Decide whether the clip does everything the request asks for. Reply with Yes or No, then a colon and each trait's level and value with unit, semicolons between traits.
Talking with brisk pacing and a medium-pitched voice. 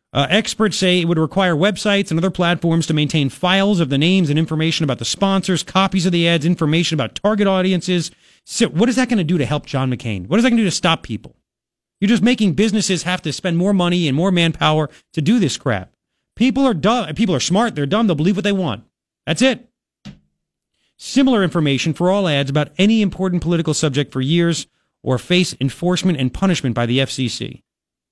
Yes: fast, 215 wpm; medium, 175 Hz